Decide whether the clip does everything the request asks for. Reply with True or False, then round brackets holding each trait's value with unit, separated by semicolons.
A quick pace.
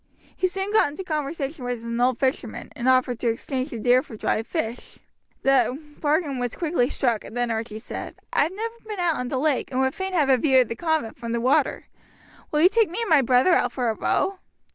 True (235 wpm)